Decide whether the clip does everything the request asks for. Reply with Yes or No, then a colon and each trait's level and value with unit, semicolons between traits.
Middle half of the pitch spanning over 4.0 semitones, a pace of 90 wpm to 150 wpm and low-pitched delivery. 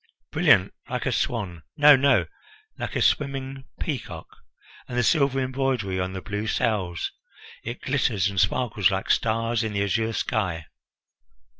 Yes: average, 5.2 semitones; average, 145 wpm; low, 115 Hz